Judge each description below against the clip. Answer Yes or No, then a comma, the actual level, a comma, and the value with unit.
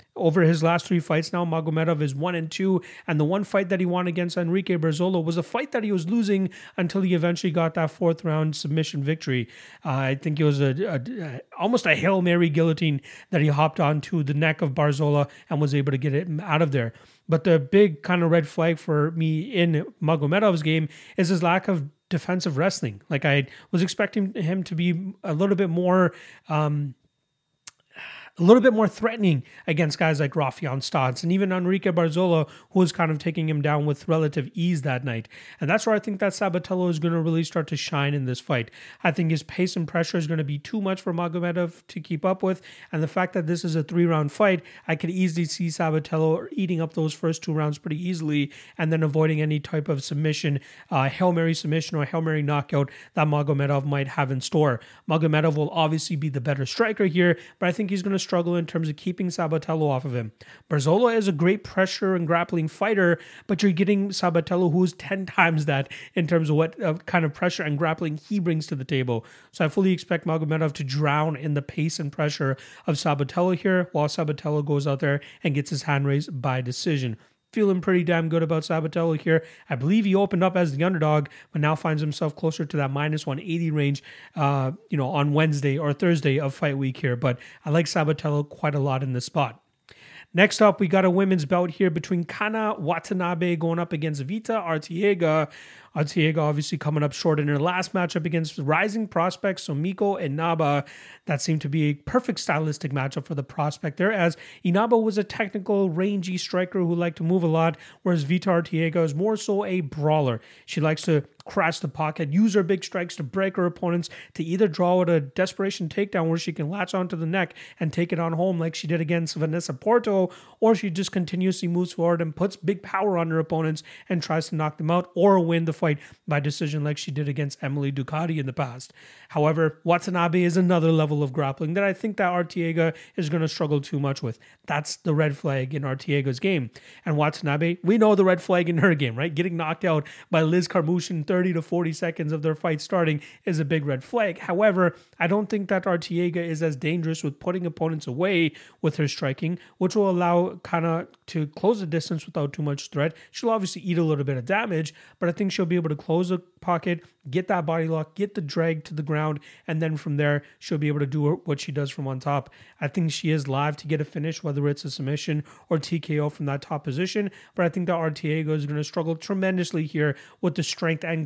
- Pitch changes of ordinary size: Yes, average, 3.2 semitones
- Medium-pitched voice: Yes, medium, 165 Hz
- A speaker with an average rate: No, fast, 220 wpm